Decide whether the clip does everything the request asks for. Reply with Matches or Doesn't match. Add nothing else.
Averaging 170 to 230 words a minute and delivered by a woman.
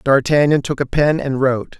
Doesn't match